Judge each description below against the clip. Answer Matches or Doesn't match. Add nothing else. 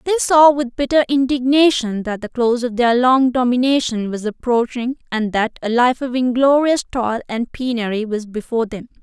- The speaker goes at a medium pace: Matches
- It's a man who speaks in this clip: Doesn't match